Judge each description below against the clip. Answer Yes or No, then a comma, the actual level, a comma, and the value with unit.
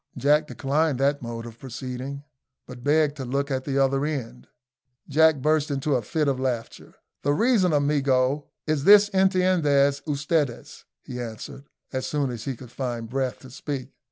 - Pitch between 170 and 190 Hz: No, medium, 140 Hz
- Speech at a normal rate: Yes, average, 165 wpm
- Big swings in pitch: No, average, 2.8 semitones